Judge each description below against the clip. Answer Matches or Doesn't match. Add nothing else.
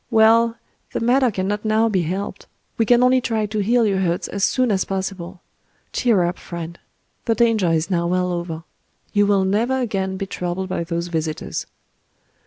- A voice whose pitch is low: Doesn't match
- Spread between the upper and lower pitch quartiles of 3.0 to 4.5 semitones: Matches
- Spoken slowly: Doesn't match